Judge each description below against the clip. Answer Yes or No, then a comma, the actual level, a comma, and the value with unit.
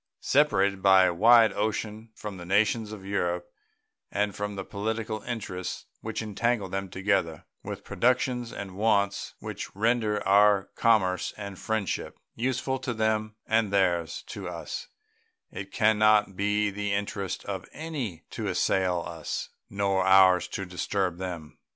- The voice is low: Yes, low, 100 Hz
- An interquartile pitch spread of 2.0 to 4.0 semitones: Yes, narrow, 2.4 semitones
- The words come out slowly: No, average, 145 wpm